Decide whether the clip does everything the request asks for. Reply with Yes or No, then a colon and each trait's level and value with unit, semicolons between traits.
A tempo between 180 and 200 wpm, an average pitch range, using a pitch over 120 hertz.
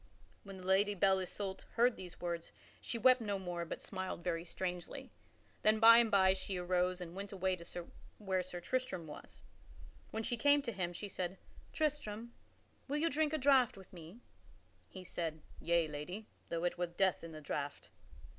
Yes: average, 185 wpm; average, 4.0 semitones; high, 190 Hz